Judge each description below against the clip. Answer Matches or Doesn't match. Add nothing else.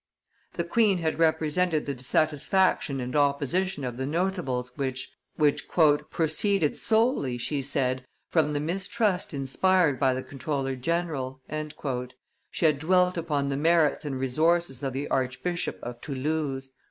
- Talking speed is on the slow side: Matches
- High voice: Doesn't match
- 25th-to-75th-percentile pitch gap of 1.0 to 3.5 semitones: Doesn't match